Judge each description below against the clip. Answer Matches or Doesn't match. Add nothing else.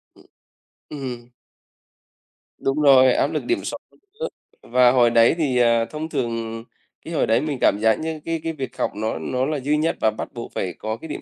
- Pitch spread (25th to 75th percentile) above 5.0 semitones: Doesn't match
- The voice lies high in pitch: Doesn't match